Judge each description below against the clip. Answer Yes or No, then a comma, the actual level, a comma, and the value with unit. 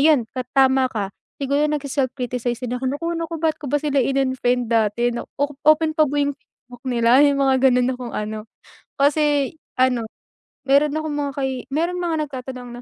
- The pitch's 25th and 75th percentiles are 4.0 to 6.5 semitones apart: No, average, 2.9 semitones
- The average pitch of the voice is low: No, very high, 270 Hz